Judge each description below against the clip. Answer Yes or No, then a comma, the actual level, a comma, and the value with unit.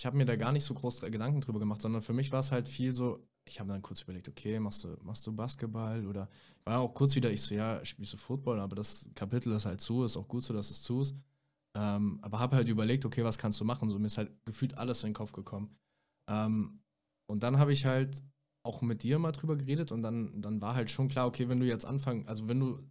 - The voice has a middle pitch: No, low, 115 Hz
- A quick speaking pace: Yes, fast, 265 wpm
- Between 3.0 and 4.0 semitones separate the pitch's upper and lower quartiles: Yes, average, 3.5 semitones